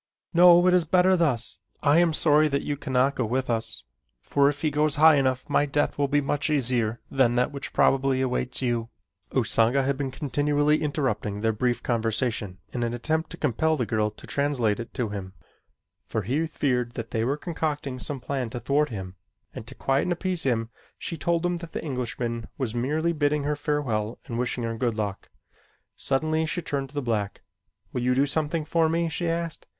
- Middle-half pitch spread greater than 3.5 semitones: Yes, average, 4.3 semitones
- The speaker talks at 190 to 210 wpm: Yes, average, 200 wpm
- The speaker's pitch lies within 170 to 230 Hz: No, low, 135 Hz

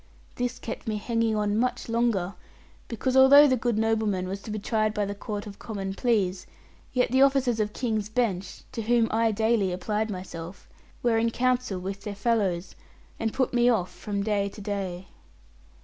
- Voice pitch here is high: Yes, high, 215 Hz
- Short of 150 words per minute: No, average, 180 wpm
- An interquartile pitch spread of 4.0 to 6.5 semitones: No, average, 2.9 semitones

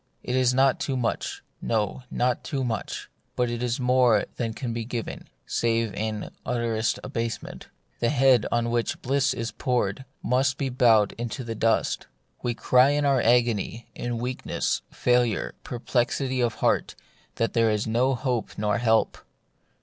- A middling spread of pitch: No, narrow, 1.9 semitones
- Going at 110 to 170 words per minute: Yes, average, 165 wpm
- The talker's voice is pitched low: Yes, low, 120 Hz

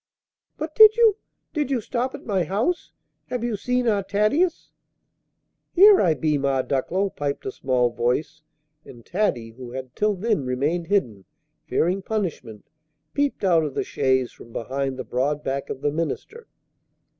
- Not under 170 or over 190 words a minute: No, average, 160 wpm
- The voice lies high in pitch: No, medium, 165 Hz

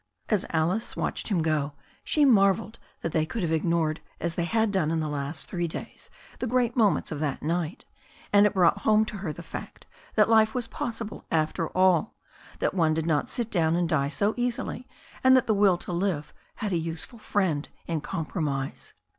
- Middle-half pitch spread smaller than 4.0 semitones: No, average, 5.1 semitones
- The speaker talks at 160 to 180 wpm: No, average, 195 wpm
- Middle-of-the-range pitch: Yes, medium, 175 Hz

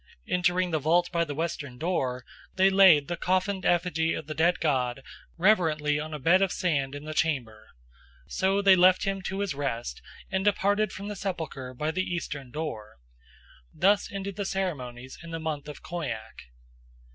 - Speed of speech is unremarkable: Yes, average, 175 wpm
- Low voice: No, medium, 165 Hz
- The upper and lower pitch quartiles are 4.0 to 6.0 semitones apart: Yes, average, 4.6 semitones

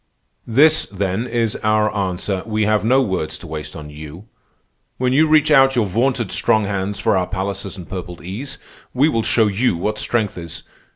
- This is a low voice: Yes, low, 105 Hz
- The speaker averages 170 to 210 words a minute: Yes, average, 185 wpm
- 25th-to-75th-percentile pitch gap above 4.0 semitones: Yes, average, 4.4 semitones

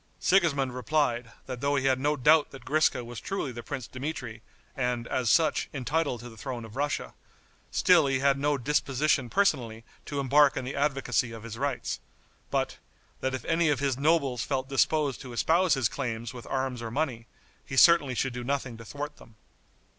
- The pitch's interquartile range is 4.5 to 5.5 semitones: No, average, 3.2 semitones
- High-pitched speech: No, low, 135 Hz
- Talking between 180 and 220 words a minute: Yes, average, 190 wpm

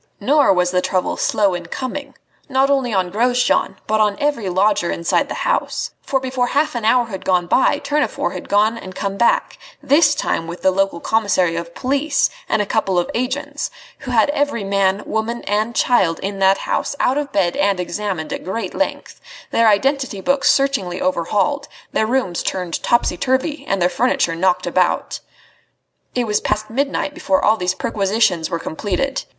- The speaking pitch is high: Yes, high, 215 Hz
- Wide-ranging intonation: Yes, wide, 5.9 semitones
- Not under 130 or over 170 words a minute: No, average, 180 wpm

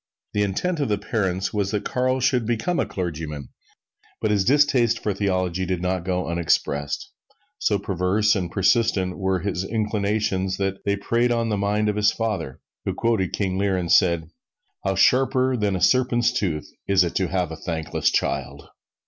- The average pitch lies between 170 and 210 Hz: No, low, 100 Hz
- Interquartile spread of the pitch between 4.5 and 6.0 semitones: No, average, 3.4 semitones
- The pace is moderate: Yes, average, 175 wpm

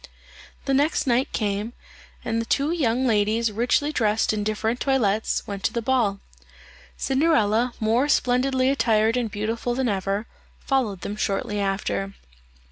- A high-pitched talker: Yes, high, 230 Hz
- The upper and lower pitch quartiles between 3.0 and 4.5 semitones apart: Yes, average, 3.8 semitones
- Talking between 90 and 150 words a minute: Yes, average, 140 wpm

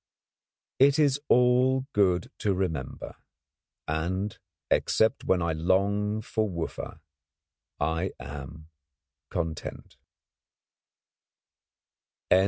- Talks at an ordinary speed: No, slow, 75 wpm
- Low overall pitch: Yes, very low, 95 Hz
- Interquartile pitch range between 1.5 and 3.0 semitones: No, average, 5.1 semitones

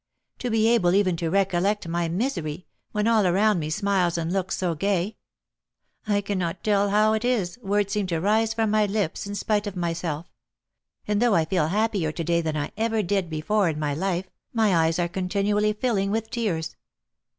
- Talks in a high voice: Yes, high, 195 Hz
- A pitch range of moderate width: Yes, average, 3.7 semitones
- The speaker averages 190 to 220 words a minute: Yes, average, 195 wpm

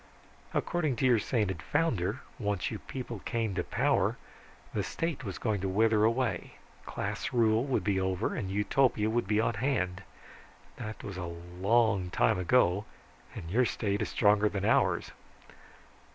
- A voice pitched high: No, low, 105 Hz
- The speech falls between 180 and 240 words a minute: No, average, 150 wpm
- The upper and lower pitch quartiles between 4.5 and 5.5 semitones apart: No, average, 3.9 semitones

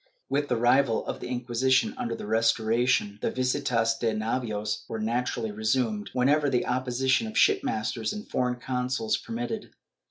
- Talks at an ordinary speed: Yes, average, 160 wpm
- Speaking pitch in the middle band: No, low, 125 Hz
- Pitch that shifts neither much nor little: Yes, average, 3.4 semitones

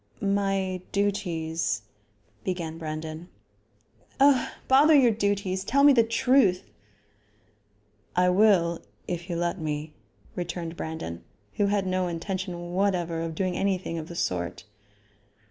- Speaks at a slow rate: Yes, slow, 125 wpm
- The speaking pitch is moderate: Yes, medium, 180 Hz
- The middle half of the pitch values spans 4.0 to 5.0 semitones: No, average, 3.4 semitones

